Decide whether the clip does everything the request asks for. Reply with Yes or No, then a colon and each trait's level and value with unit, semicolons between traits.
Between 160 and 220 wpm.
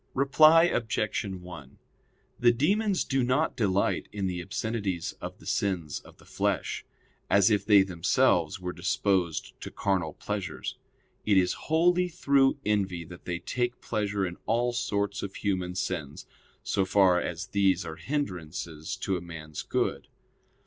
No: average, 150 wpm